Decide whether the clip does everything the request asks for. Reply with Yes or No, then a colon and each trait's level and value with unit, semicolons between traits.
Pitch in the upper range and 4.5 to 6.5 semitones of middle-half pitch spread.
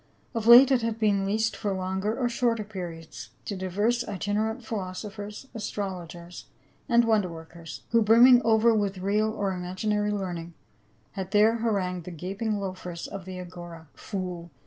No: high, 200 Hz; average, 3.4 semitones